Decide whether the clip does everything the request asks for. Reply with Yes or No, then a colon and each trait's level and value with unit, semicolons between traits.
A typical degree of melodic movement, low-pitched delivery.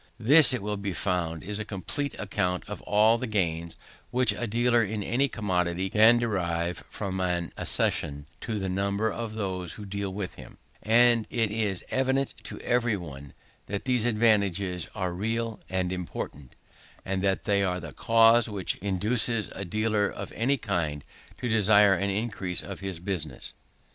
Yes: average, 3.6 semitones; low, 100 Hz